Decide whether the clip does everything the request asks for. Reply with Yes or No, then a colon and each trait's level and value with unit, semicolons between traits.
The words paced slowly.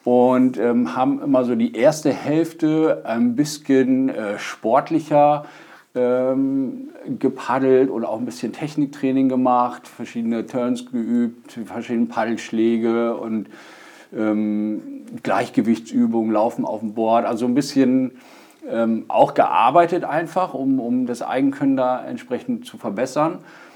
Yes: slow, 120 wpm